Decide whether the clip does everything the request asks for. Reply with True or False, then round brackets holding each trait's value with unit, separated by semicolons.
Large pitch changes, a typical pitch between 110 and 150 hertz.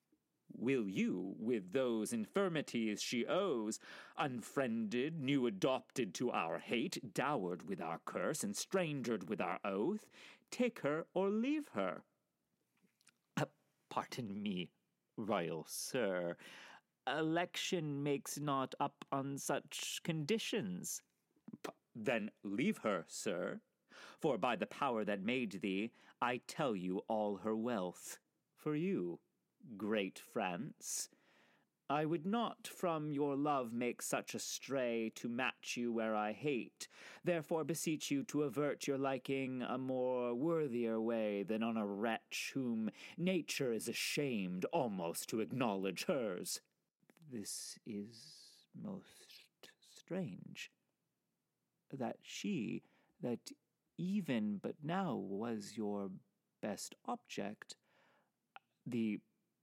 True (7.8 semitones; 140 Hz)